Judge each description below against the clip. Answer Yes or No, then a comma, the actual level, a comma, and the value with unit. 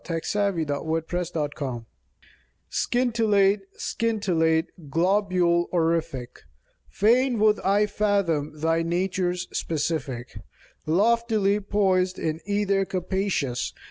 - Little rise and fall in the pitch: No, average, 4.1 semitones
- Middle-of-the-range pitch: Yes, medium, 180 Hz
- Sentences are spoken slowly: Yes, slow, 85 wpm